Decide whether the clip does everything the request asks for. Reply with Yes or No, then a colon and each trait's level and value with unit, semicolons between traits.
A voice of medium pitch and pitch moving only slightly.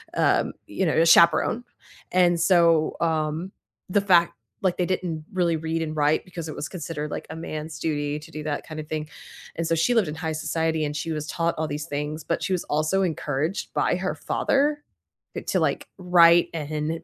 Yes: medium, 160 Hz; narrow, 2.2 semitones